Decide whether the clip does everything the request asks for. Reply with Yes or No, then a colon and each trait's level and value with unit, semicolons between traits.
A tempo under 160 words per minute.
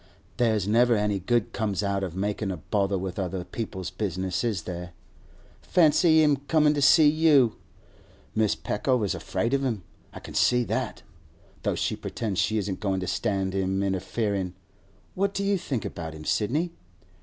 No: average, 165 wpm